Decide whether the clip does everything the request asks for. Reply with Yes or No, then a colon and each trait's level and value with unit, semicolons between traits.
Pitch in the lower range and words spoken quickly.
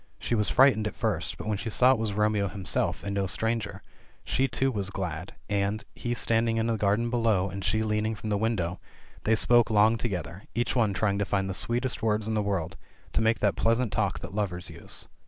Yes: low, 105 Hz; fast, 230 wpm